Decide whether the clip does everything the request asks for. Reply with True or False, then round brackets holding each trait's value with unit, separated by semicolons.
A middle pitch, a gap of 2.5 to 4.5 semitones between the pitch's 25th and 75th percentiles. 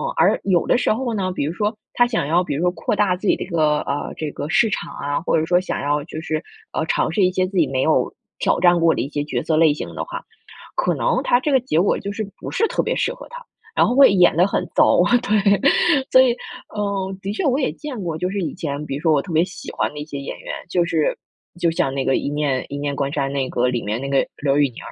False (170 Hz; 5.5 semitones)